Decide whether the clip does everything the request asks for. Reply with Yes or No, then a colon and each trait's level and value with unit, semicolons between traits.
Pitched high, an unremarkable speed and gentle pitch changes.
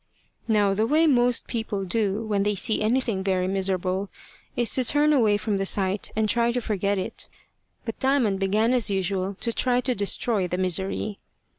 No: high, 210 Hz; average, 180 wpm; average, 3.5 semitones